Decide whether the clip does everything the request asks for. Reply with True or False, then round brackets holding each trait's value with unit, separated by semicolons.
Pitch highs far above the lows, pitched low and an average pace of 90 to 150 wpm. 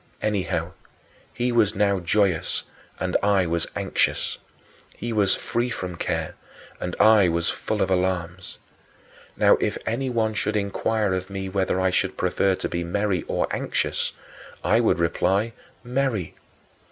False (3.2 semitones; 100 Hz; 140 wpm)